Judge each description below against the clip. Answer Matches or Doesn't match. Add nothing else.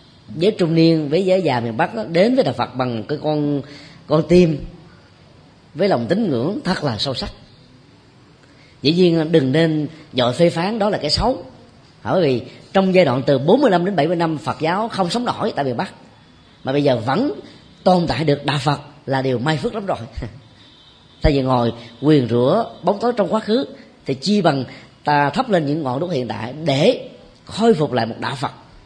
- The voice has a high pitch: Doesn't match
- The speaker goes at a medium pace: Matches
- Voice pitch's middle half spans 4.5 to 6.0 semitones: Matches